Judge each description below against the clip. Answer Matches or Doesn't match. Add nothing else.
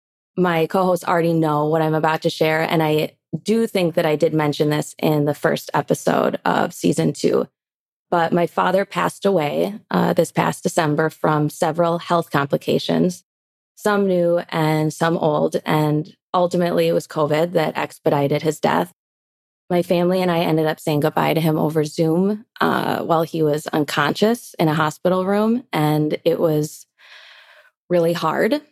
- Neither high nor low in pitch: Matches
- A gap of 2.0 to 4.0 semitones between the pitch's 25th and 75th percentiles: Matches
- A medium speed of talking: Matches